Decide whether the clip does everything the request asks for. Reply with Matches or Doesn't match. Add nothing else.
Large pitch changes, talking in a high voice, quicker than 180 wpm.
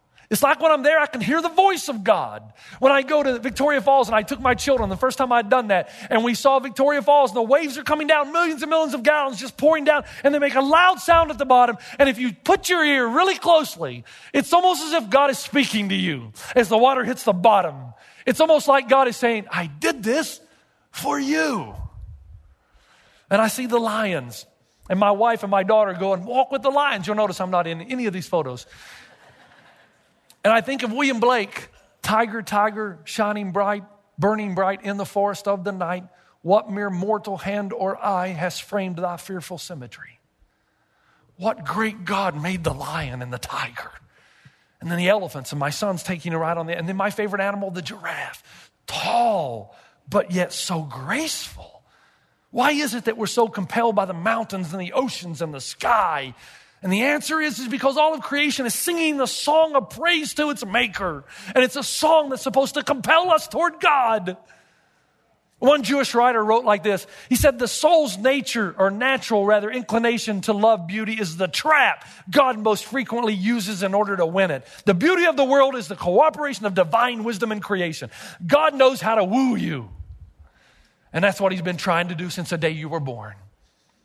Matches